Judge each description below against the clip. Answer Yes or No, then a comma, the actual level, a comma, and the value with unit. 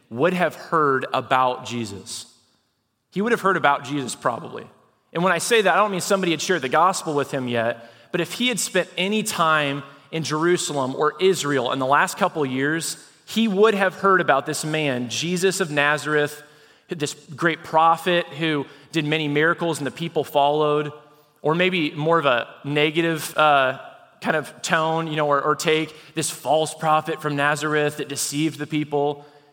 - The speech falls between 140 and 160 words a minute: No, average, 185 wpm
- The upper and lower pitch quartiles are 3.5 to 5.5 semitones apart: No, average, 2.7 semitones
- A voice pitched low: No, medium, 155 Hz